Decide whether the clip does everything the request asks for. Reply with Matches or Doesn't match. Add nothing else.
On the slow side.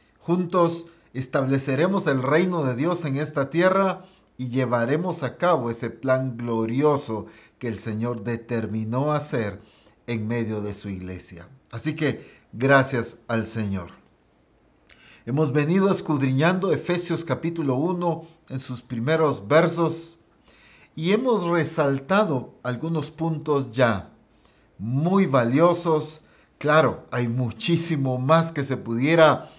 Matches